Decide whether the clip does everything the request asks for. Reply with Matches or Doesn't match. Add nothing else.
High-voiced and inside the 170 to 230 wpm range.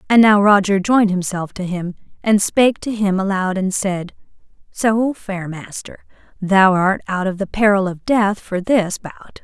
Matches